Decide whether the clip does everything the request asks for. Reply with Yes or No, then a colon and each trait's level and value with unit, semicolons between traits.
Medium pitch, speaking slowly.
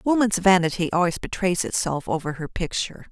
No: medium, 180 Hz; average, 155 wpm